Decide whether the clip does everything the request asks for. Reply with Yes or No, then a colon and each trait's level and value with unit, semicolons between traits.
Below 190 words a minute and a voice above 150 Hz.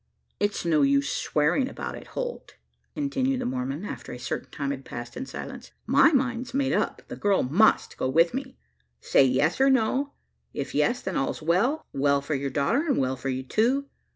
No: average, 195 wpm; medium, 185 Hz